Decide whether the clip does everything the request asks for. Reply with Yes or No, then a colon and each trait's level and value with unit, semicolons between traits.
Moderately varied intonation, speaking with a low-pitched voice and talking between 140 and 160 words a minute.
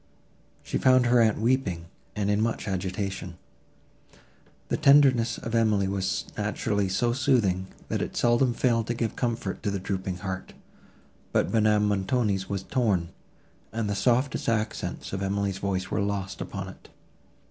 Yes: average, 3.6 semitones; low, 105 Hz; average, 150 wpm